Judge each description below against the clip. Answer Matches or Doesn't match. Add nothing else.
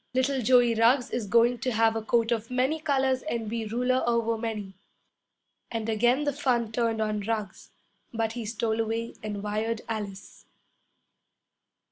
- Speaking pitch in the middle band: Doesn't match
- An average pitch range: Doesn't match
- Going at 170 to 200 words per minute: Doesn't match